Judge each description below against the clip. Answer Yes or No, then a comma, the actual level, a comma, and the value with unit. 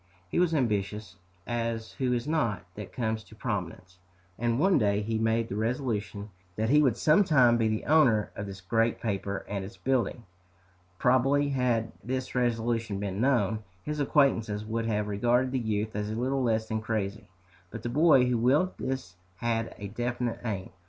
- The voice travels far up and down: No, average, 3.3 semitones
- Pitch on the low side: Yes, low, 115 Hz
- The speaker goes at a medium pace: Yes, average, 170 wpm